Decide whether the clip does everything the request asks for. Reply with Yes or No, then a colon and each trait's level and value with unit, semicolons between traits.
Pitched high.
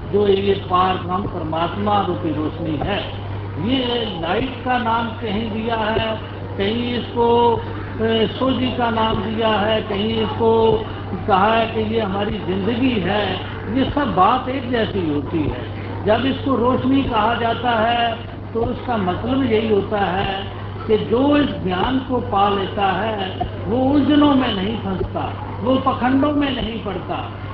Yes: high, 220 Hz